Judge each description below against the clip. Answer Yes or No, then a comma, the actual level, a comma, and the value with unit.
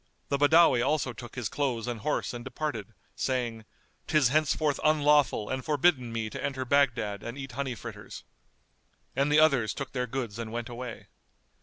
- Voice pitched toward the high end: No, low, 130 Hz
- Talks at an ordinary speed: Yes, average, 170 wpm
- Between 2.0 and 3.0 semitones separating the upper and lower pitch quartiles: No, average, 3.4 semitones